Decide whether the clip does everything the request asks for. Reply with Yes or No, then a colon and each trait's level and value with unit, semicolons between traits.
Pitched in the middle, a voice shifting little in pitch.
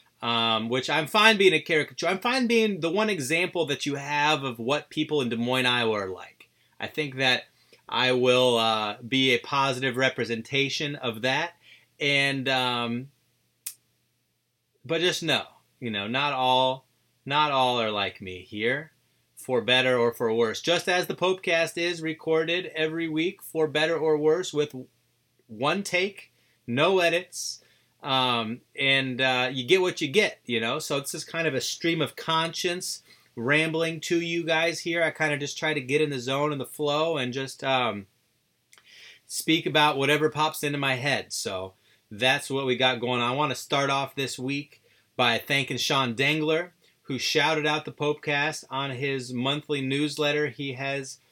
No: medium, 145 Hz; average, 4.0 semitones